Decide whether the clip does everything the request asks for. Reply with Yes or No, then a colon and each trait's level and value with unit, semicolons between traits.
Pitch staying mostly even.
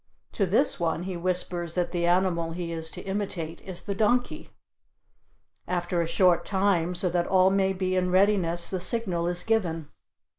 Yes: narrow, 2.0 semitones